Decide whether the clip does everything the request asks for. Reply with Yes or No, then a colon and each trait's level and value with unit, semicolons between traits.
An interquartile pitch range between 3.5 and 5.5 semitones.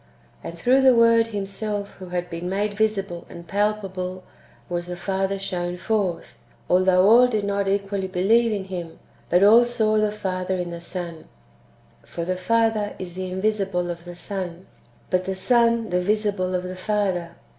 No: average, 2.8 semitones